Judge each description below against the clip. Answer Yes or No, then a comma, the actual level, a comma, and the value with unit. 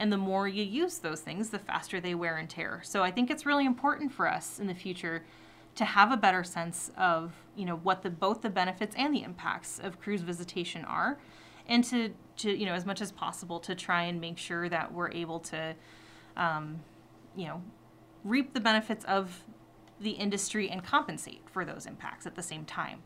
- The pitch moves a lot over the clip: No, average, 4.0 semitones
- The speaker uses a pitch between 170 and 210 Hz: Yes, medium, 185 Hz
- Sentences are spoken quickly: Yes, fast, 210 wpm